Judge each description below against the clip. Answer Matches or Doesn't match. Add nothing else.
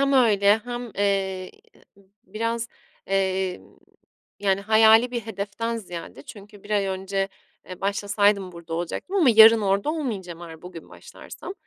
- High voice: Matches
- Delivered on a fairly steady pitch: Doesn't match